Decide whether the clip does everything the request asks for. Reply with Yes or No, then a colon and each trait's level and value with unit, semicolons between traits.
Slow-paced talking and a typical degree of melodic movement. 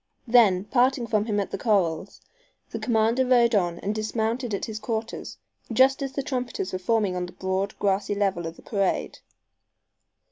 No: average, 175 wpm; average, 3.7 semitones